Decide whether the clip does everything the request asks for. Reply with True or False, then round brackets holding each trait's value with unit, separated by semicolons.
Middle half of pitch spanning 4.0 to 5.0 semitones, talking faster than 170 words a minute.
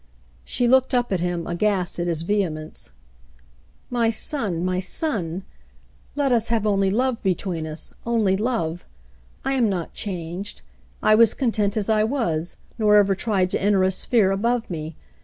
False (4.5 semitones; 165 wpm)